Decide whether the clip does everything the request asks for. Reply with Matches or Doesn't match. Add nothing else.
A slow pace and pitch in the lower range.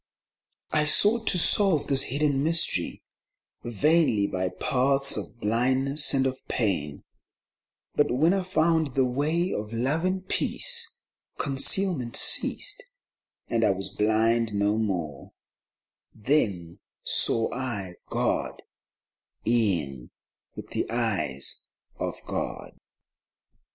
Matches